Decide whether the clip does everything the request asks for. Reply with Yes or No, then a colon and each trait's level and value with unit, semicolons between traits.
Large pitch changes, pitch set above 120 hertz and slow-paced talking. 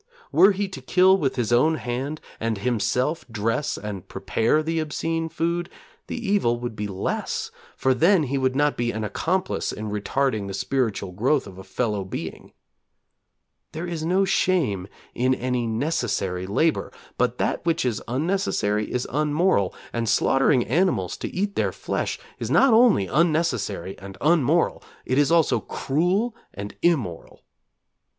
No: wide, 7.3 semitones; low, 135 Hz; average, 155 wpm